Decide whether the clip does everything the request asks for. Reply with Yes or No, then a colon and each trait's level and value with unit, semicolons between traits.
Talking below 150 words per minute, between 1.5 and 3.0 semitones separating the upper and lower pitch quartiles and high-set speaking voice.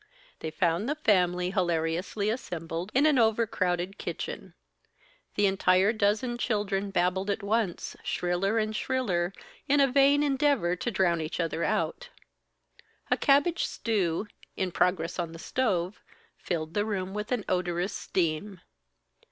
No: average, 140 wpm; average, 4.3 semitones; high, 195 Hz